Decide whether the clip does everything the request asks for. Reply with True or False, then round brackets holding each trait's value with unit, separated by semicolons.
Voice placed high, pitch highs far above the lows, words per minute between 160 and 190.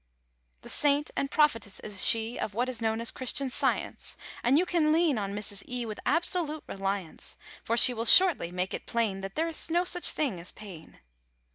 False (235 Hz; 7.0 semitones; 200 wpm)